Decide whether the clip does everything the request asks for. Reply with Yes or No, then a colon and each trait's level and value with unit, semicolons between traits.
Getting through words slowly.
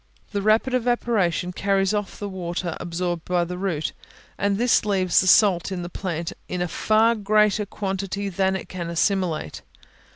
No: average, 165 wpm